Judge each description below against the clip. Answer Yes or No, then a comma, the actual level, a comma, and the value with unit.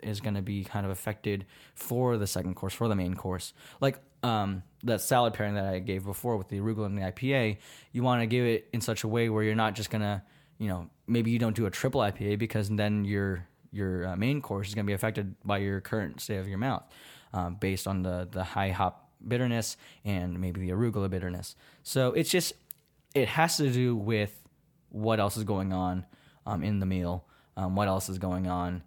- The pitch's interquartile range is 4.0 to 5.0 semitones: No, average, 3.5 semitones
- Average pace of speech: No, fast, 225 wpm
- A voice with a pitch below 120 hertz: Yes, low, 105 Hz